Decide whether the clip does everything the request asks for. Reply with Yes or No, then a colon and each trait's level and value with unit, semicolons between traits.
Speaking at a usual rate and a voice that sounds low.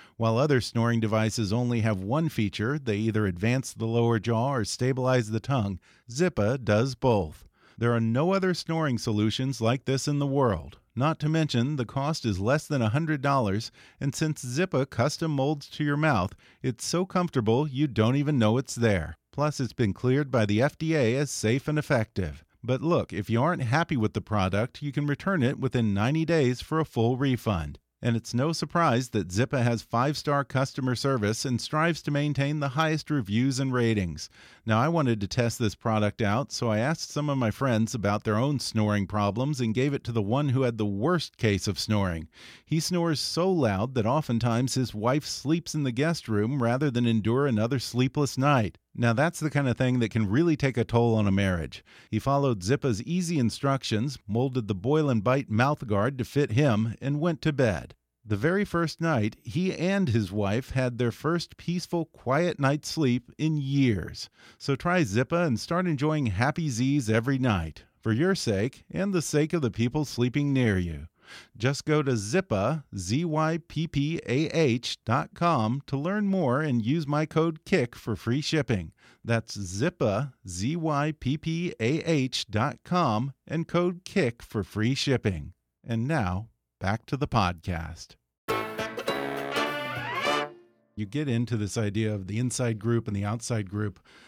Yes: average, 185 wpm; low, 125 Hz